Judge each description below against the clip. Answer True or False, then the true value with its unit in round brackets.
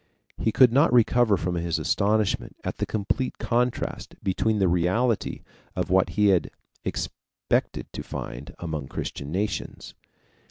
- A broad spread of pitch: False (4.8 semitones)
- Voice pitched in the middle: False (100 Hz)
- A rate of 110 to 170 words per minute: True (135 wpm)